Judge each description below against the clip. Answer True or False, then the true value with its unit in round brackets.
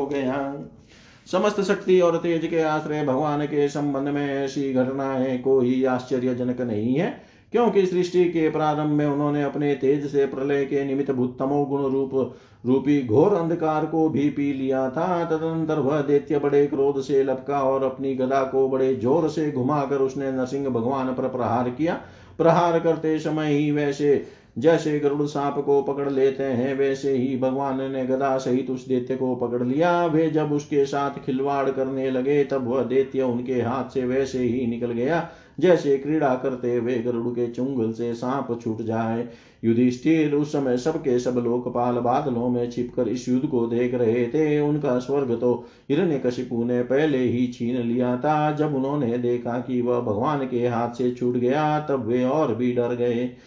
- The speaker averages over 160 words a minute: True (175 wpm)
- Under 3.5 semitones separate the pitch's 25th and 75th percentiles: True (2.8 semitones)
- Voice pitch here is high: False (135 Hz)